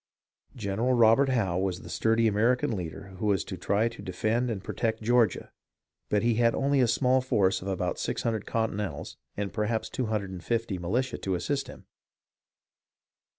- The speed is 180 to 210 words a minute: No, average, 155 wpm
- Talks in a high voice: No, low, 110 Hz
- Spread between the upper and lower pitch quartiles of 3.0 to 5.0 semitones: Yes, average, 3.5 semitones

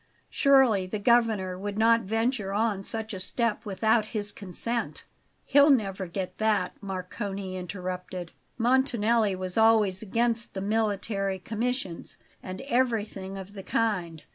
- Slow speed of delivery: Yes, slow, 130 wpm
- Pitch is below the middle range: No, high, 210 Hz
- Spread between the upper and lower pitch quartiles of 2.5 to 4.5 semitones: Yes, average, 3.3 semitones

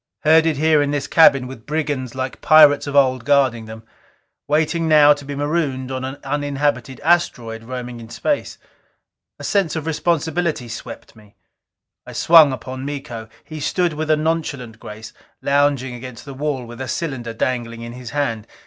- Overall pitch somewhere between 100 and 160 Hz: Yes, medium, 140 Hz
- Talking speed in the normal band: Yes, average, 165 wpm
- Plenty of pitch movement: No, average, 3.7 semitones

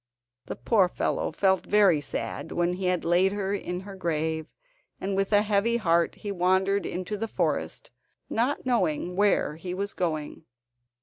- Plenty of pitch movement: No, average, 2.8 semitones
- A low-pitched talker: No, high, 190 Hz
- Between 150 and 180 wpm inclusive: Yes, average, 165 wpm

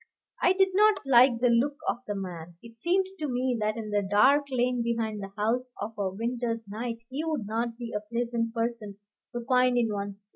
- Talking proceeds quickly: Yes, fast, 215 wpm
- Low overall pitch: No, high, 235 Hz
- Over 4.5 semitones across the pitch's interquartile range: No, average, 3.1 semitones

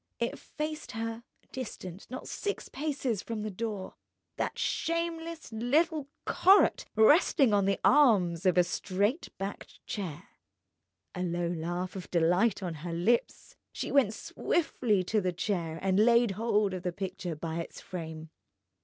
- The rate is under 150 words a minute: Yes, average, 140 wpm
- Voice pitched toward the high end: Yes, high, 205 Hz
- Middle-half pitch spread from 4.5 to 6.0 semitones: Yes, wide, 5.5 semitones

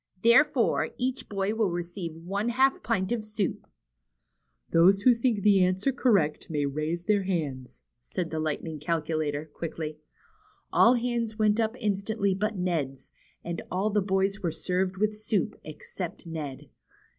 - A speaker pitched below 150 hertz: No, high, 190 Hz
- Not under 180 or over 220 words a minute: No, average, 145 wpm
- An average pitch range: Yes, average, 4.9 semitones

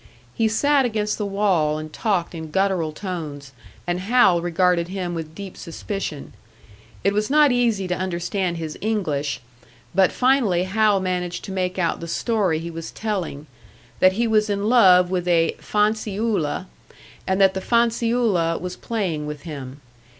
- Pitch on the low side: No, medium, 185 Hz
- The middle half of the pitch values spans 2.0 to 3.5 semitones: No, average, 4.0 semitones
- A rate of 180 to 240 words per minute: No, average, 155 wpm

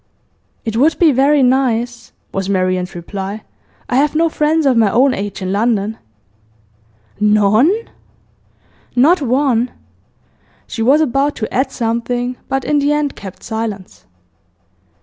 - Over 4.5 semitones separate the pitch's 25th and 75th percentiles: Yes, average, 5.1 semitones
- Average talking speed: No, slow, 130 wpm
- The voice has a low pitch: No, high, 245 Hz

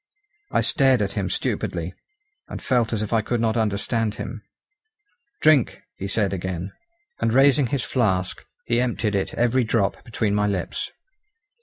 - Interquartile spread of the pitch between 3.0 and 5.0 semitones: Yes, average, 3.4 semitones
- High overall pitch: No, low, 110 Hz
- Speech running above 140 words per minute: Yes, average, 155 wpm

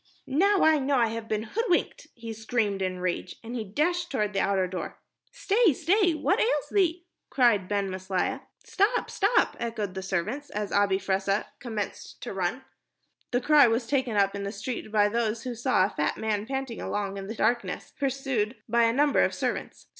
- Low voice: No, high, 230 Hz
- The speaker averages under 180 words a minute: No, average, 190 wpm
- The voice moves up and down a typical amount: No, wide, 5.7 semitones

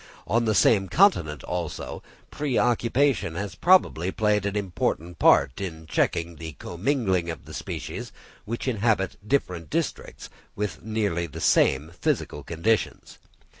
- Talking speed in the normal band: No, slow, 130 wpm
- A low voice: Yes, very low, 95 Hz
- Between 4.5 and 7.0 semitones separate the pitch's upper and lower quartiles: Yes, average, 5.2 semitones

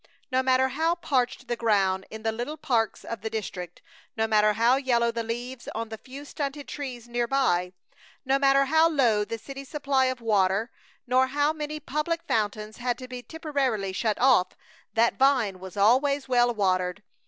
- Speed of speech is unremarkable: Yes, average, 180 wpm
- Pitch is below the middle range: No, high, 245 Hz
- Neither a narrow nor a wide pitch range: Yes, average, 3.9 semitones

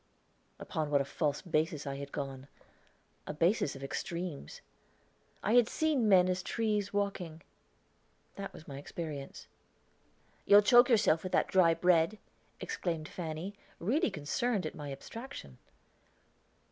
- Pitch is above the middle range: No, medium, 170 Hz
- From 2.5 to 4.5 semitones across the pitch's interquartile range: No, wide, 5.6 semitones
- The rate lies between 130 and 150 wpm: Yes, slow, 135 wpm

